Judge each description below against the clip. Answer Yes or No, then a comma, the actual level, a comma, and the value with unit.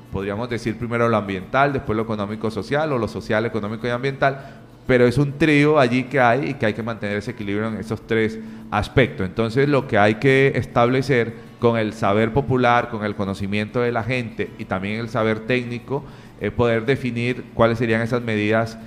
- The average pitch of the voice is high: No, low, 115 Hz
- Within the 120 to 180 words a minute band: No, fast, 190 wpm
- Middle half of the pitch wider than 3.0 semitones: No, narrow, 2.5 semitones